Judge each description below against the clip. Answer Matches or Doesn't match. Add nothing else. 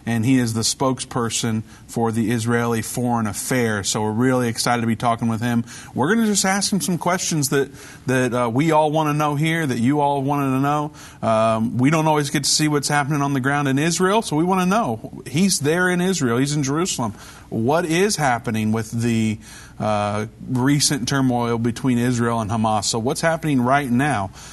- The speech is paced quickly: Matches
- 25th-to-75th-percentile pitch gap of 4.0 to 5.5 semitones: Matches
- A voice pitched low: Matches